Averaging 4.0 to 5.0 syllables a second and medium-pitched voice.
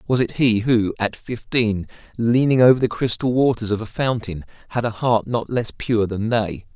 No: 4.8 syllables/s; low, 115 Hz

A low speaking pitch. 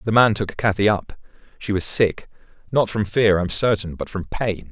Yes: low, 100 Hz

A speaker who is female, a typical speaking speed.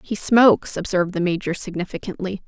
Yes: female; average, 145 wpm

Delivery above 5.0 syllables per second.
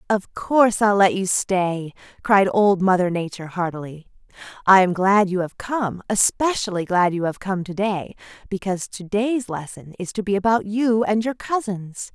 No: 4.7 syllables/s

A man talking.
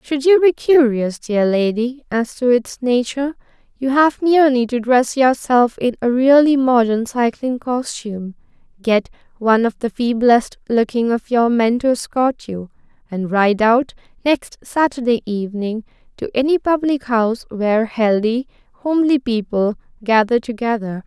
No: female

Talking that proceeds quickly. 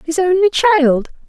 No: average, 140 wpm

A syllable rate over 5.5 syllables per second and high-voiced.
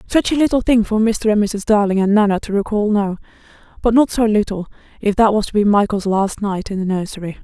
Yes: 5.9 syllables/s; high, 210 Hz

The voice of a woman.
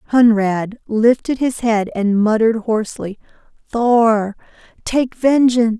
Yes: female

